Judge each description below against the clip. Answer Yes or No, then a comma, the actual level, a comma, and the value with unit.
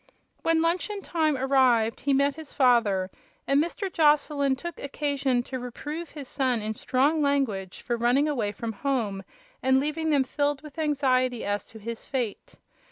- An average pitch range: Yes, average, 3.7 semitones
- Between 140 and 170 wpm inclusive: Yes, average, 165 wpm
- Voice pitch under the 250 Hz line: No, very high, 270 Hz